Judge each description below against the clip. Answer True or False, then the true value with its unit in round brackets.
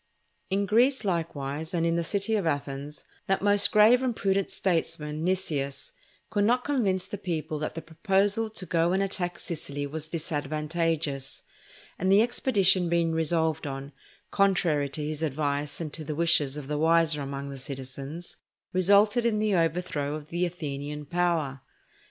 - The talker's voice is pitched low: False (165 Hz)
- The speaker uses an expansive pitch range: False (4.6 semitones)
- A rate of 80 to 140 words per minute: False (160 wpm)